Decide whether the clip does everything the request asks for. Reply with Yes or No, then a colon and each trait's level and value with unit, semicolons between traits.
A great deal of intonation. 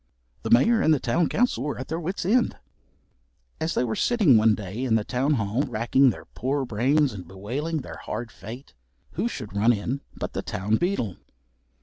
Yes: wide, 6.0 semitones